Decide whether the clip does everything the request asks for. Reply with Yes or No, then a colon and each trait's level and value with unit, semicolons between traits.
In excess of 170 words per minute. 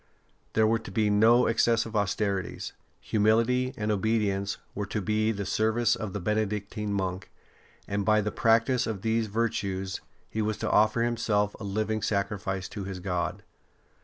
No: average, 160 wpm